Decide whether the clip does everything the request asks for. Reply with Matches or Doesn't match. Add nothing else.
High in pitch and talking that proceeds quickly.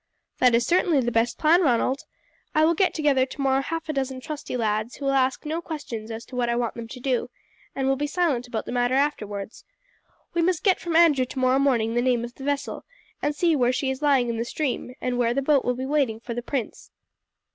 Matches